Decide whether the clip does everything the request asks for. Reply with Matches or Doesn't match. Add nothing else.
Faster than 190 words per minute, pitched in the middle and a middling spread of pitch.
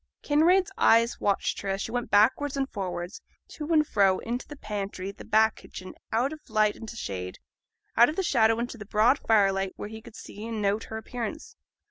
Doesn't match